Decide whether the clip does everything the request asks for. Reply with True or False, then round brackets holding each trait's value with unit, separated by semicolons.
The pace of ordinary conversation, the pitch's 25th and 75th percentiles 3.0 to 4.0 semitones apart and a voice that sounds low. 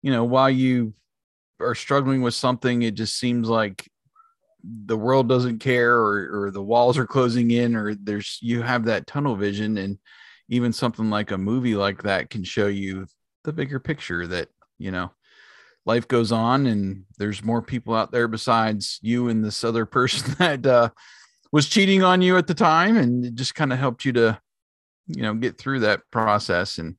True (190 wpm; 3.4 semitones; 120 Hz)